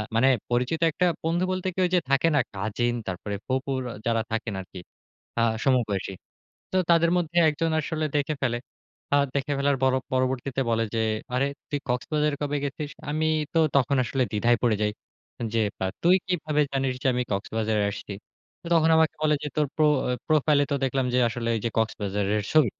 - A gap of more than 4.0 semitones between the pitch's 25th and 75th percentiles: Yes, average, 4.9 semitones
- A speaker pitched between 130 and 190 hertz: Yes, low, 135 Hz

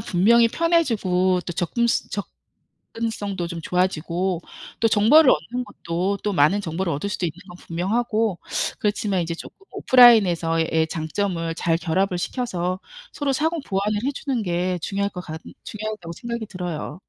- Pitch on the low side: No, high, 190 Hz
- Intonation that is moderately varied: Yes, average, 4.6 semitones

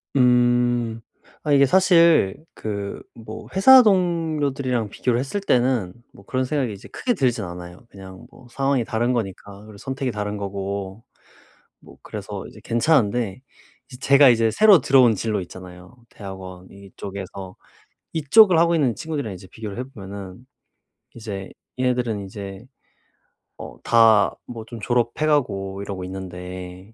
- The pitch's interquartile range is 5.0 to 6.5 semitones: Yes, wide, 5.4 semitones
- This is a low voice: Yes, low, 115 Hz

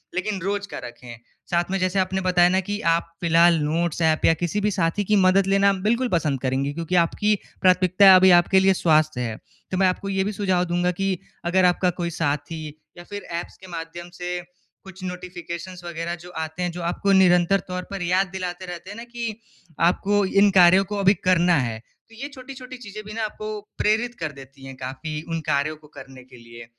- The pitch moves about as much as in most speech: Yes, average, 3.0 semitones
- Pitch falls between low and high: Yes, medium, 180 Hz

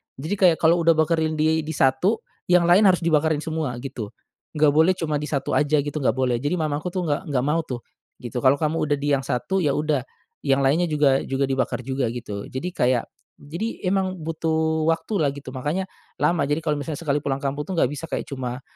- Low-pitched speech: No, medium, 150 Hz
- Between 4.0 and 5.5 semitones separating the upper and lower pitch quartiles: No, average, 3.2 semitones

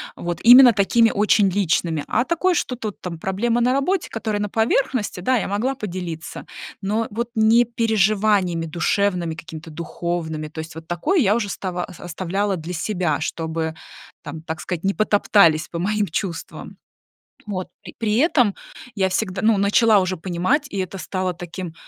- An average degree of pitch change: Yes, average, 4.3 semitones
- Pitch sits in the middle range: No, high, 195 Hz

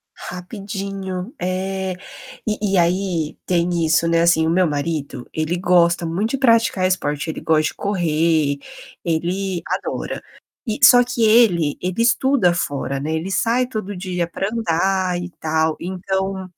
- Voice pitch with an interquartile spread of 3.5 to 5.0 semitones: No, average, 3.0 semitones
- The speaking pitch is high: No, medium, 180 Hz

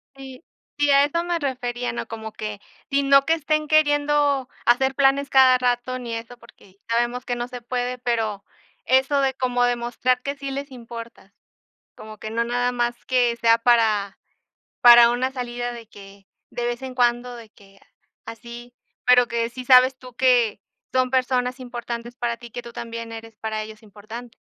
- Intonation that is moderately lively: No, narrow, 1.9 semitones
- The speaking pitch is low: No, high, 245 Hz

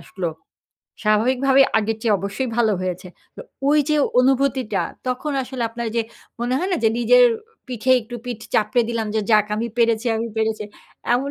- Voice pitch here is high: Yes, high, 235 Hz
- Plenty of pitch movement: No, average, 3.3 semitones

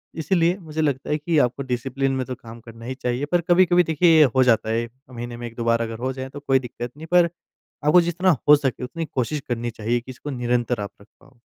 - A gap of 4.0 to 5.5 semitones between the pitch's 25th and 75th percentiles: Yes, average, 4.5 semitones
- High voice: No, low, 130 Hz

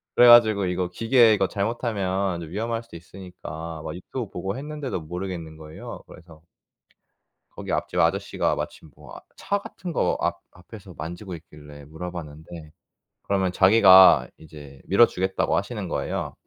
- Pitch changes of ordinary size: Yes, average, 4.9 semitones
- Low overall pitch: Yes, very low, 95 Hz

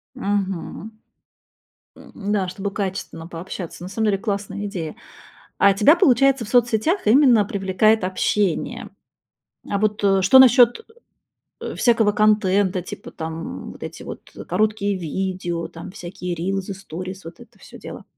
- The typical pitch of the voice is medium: No, high, 200 Hz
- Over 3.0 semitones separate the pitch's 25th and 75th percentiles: No, average, 2.7 semitones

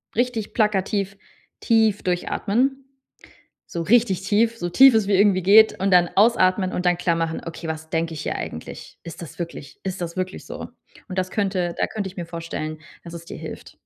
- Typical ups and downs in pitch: Yes, average, 3.8 semitones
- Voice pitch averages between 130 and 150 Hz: No, medium, 185 Hz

